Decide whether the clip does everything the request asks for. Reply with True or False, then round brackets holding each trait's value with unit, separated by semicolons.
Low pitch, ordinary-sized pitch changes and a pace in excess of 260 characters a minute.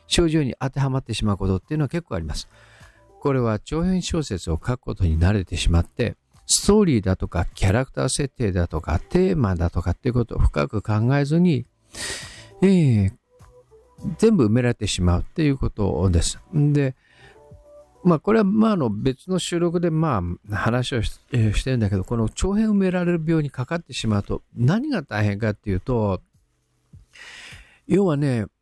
False (120 Hz; 8.7 semitones; 345 characters per minute)